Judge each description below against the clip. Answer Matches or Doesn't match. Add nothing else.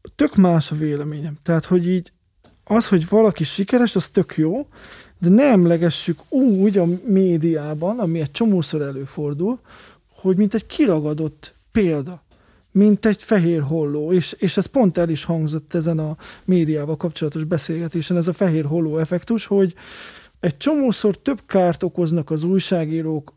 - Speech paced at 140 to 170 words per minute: Matches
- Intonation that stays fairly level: Doesn't match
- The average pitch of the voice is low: Doesn't match